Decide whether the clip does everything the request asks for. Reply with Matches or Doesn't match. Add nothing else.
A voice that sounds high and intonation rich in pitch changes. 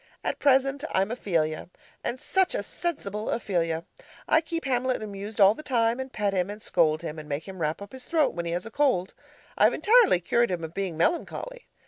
Matches